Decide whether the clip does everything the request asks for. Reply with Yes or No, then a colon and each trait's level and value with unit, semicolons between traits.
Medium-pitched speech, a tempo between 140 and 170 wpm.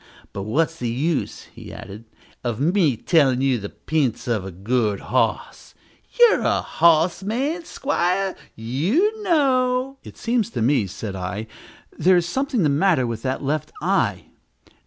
Yes: medium, 155 Hz; average, 155 wpm